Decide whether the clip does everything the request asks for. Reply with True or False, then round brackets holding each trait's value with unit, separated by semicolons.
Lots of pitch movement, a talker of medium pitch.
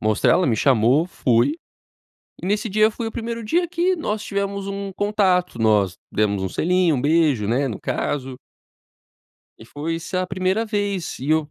True (7.8 semitones; 180 Hz)